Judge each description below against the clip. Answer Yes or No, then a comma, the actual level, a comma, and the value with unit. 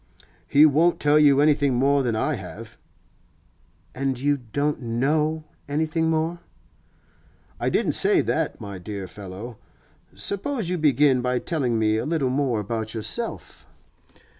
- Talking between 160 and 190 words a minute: No, average, 140 wpm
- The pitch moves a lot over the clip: No, average, 4.8 semitones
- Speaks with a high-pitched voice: No, medium, 140 Hz